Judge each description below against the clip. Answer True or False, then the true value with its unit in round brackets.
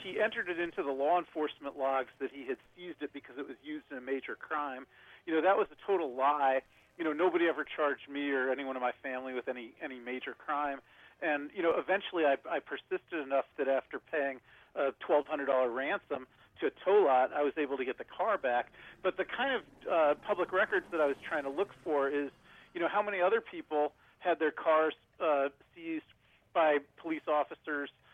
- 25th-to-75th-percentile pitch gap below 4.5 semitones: True (3.9 semitones)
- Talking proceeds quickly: True (210 wpm)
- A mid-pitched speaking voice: True (145 Hz)